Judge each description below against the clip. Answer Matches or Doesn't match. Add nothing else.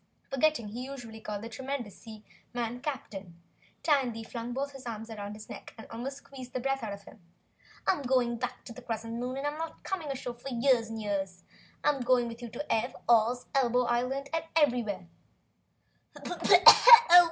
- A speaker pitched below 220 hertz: Doesn't match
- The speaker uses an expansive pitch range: Doesn't match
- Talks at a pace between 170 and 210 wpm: Matches